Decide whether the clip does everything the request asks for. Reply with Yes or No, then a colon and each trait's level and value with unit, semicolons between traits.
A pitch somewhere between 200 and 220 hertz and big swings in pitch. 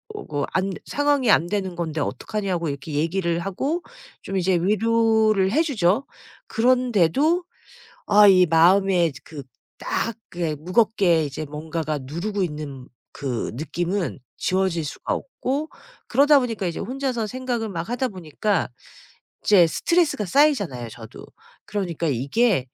No: high, 190 Hz; wide, 6.1 semitones